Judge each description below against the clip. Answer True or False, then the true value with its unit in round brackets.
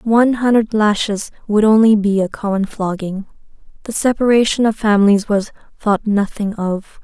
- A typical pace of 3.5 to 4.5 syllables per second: False (4.9 syllables/s)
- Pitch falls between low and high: False (210 Hz)